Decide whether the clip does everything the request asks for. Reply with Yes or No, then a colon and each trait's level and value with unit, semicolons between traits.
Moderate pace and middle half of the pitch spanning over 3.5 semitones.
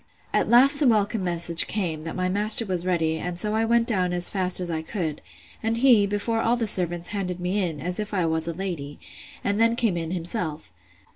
No: fast, 220 wpm; average, 4.2 semitones